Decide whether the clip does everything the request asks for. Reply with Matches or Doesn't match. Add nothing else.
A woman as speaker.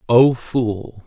Doesn't match